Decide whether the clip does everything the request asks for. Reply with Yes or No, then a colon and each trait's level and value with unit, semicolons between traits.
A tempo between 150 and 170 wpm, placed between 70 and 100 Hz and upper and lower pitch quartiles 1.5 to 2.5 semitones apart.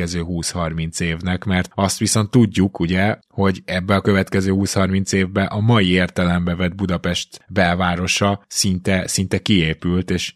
No: average, 135 wpm; very low, 95 Hz; narrow, 1.9 semitones